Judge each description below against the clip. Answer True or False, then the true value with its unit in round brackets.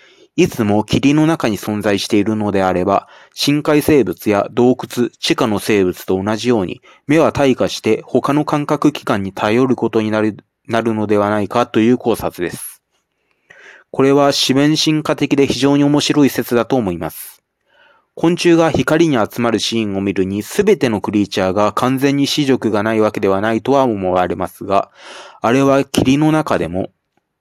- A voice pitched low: True (120 Hz)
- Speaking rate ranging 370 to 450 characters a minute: False (325 characters per minute)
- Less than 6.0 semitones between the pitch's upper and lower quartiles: True (5.3 semitones)